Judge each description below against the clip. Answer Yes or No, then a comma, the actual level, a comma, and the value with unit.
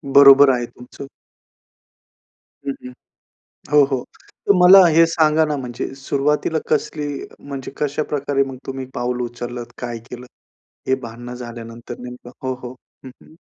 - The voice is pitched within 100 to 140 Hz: Yes, low, 135 Hz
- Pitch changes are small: No, average, 3.1 semitones